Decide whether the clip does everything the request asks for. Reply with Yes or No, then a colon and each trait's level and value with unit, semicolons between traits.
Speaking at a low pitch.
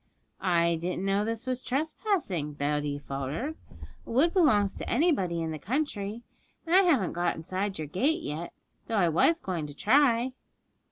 No: high, 200 Hz